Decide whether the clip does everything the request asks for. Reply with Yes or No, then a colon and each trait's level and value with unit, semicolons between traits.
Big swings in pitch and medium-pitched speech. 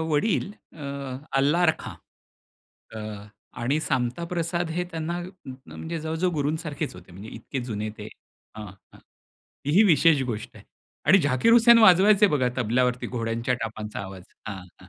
Yes: wide, 6.7 semitones; medium, 145 Hz